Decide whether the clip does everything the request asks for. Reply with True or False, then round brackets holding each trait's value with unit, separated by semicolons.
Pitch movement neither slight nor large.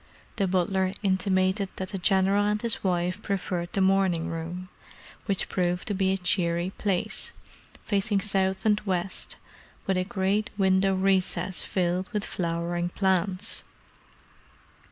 False (1.5 semitones)